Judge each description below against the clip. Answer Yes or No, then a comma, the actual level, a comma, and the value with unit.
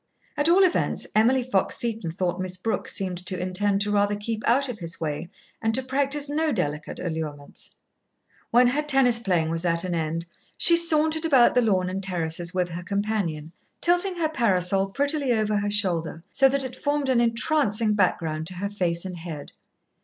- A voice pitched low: No, high, 205 Hz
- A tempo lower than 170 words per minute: No, average, 185 wpm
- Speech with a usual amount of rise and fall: No, wide, 6.9 semitones